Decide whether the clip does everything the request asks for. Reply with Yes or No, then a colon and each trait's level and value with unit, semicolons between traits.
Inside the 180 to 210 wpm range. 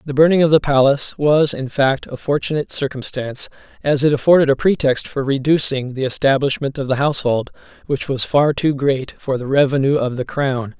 Yes: average, 190 wpm